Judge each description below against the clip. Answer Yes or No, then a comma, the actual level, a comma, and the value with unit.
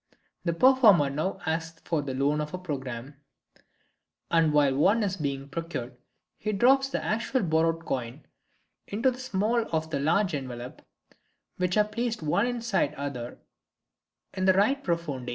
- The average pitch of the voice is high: No, medium, 165 Hz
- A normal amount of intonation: No, wide, 6.8 semitones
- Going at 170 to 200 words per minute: No, average, 155 wpm